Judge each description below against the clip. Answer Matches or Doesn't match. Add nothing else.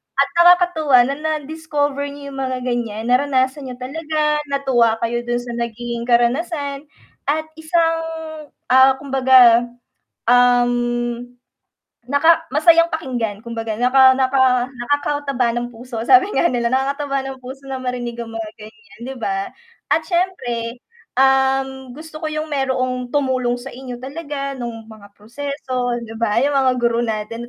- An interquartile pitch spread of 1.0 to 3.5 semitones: Matches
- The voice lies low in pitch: Doesn't match